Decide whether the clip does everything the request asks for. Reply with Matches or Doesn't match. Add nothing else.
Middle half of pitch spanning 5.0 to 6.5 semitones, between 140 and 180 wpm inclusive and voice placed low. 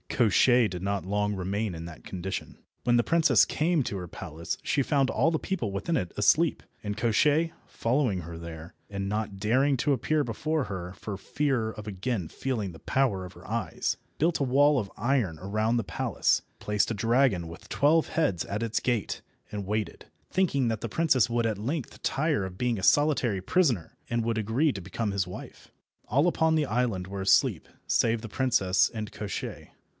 Doesn't match